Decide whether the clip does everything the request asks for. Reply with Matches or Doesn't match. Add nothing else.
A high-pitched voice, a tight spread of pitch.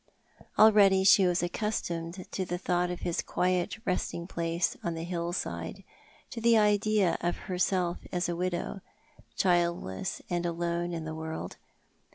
Doesn't match